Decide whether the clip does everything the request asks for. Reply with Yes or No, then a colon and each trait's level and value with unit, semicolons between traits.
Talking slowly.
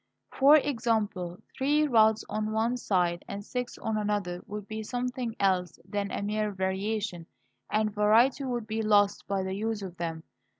No: average, 165 wpm